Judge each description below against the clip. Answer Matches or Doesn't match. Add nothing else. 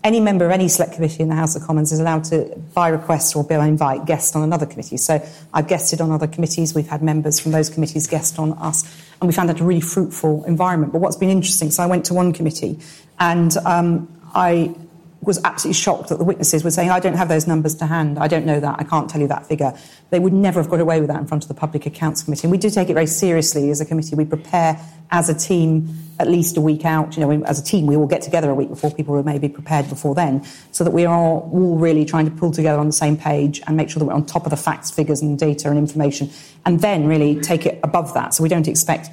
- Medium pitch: Matches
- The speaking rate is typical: Doesn't match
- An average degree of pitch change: Doesn't match